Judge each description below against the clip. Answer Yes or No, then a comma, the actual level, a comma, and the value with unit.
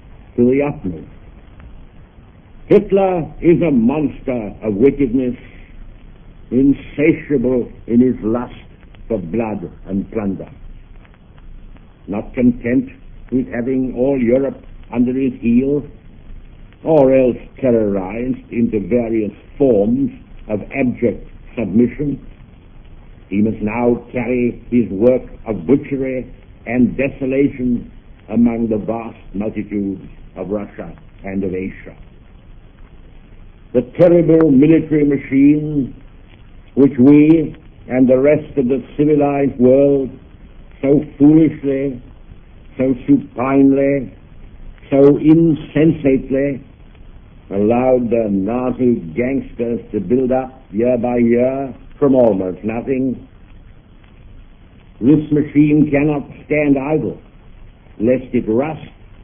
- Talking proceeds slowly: Yes, slow, 95 wpm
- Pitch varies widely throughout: No, average, 4.4 semitones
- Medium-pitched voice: No, low, 125 Hz